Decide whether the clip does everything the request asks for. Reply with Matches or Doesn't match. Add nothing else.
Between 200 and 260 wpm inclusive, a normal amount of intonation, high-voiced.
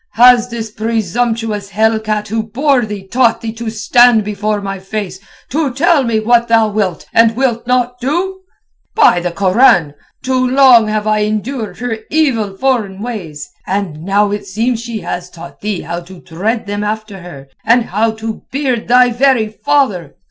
Doesn't match